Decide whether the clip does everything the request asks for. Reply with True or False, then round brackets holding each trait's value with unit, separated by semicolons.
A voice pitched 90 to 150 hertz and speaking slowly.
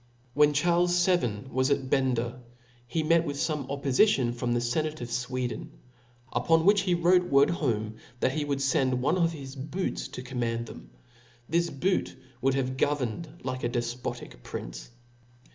False (135 Hz; 160 wpm)